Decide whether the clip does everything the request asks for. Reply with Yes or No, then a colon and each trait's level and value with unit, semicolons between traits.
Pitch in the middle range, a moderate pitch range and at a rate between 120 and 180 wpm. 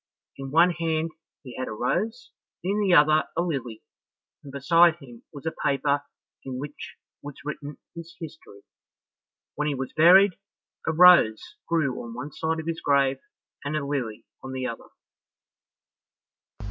Yes: medium, 150 Hz; average, 3.8 semitones; average, 155 wpm